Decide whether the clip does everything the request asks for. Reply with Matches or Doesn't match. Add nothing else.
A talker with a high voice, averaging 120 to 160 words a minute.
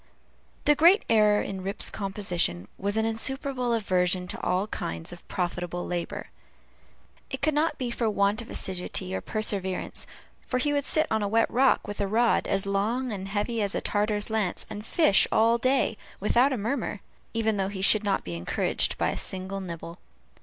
Doesn't match